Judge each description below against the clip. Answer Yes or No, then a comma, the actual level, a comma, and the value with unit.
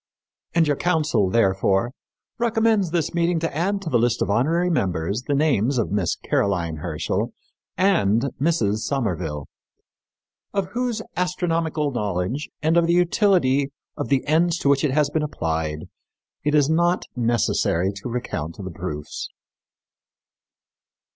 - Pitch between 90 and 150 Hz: Yes, medium, 140 Hz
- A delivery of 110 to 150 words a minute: Yes, average, 140 wpm